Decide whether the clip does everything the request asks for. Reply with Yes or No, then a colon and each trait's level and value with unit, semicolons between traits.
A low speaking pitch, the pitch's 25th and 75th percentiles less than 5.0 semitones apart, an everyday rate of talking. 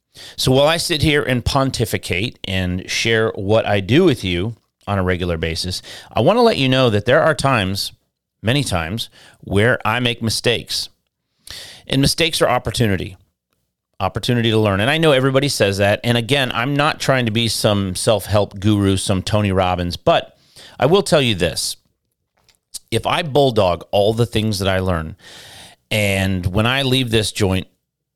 No: low, 110 Hz; wide, 5.4 semitones; average, 175 wpm